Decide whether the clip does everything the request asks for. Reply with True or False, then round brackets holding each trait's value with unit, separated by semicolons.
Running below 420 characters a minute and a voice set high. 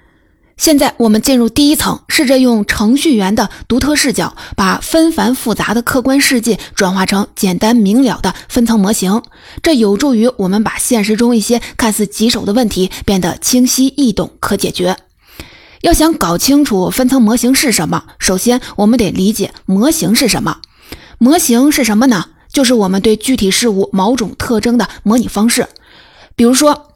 True (270 characters per minute; 235 Hz)